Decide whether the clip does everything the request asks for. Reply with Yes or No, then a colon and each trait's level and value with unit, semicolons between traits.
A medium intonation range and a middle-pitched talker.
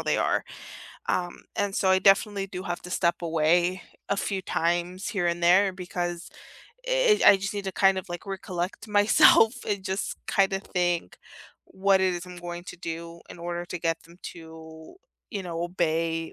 No: narrow, 2.1 semitones; medium, 180 Hz